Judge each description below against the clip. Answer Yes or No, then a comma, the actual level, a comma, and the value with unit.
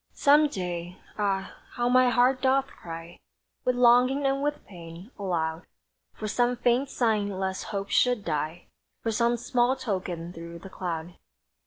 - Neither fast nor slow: Yes, average, 150 wpm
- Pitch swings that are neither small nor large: No, wide, 6.0 semitones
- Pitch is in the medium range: No, high, 210 Hz